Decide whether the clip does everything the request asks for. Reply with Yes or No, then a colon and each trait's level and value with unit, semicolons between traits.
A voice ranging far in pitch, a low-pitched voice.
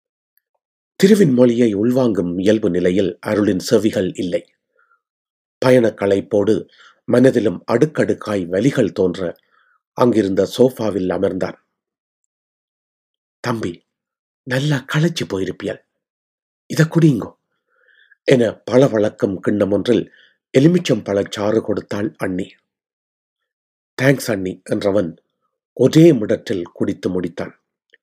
Yes: wide, 8.2 semitones; low, 125 Hz